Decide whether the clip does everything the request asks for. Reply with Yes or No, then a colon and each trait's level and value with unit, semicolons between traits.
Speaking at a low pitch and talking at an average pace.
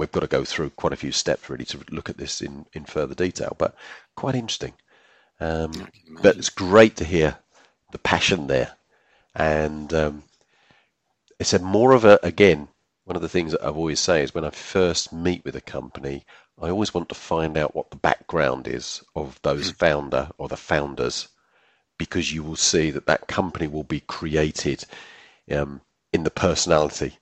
Yes: very low, 80 Hz; average, 185 wpm